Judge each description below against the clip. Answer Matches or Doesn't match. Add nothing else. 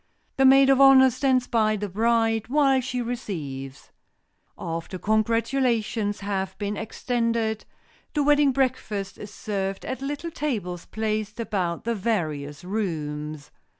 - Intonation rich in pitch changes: Doesn't match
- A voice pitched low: Doesn't match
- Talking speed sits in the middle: Doesn't match